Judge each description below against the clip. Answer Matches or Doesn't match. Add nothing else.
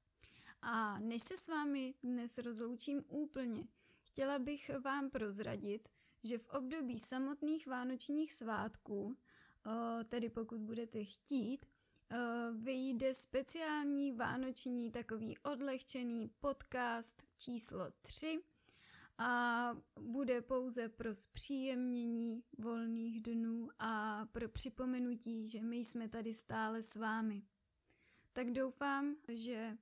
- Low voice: Doesn't match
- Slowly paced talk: Matches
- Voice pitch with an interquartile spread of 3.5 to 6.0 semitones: Doesn't match